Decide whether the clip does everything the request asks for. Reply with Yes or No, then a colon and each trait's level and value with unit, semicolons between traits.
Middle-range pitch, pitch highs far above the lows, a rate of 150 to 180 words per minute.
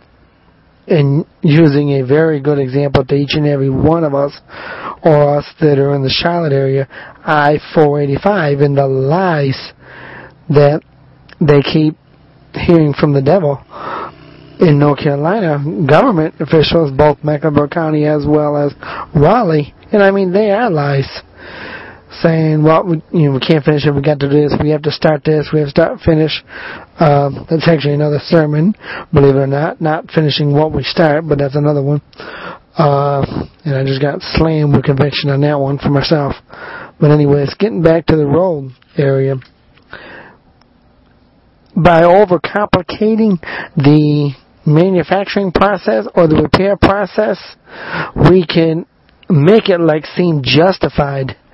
No: medium, 150 Hz; narrow, 2.6 semitones; average, 155 wpm